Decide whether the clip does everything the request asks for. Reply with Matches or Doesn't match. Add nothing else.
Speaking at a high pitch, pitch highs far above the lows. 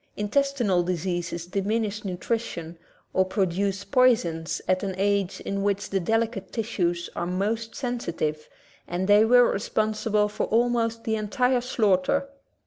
Doesn't match